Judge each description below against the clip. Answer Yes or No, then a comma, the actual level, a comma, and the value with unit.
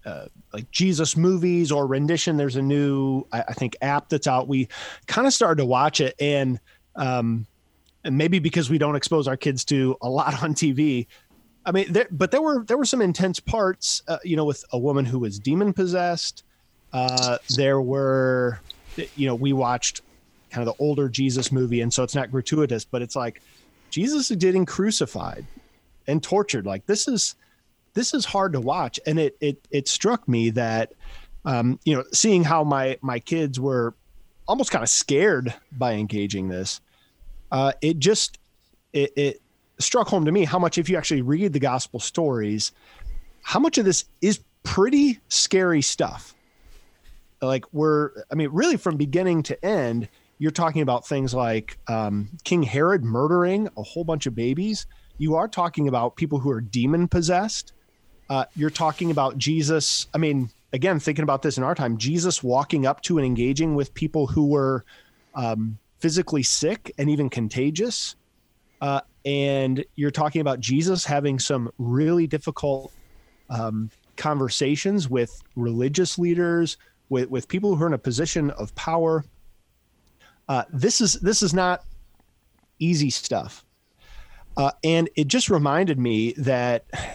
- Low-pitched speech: No, medium, 145 Hz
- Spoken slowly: No, average, 170 wpm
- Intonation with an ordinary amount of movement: Yes, average, 4.9 semitones